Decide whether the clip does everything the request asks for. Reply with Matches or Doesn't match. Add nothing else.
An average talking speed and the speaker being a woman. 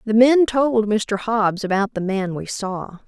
Matches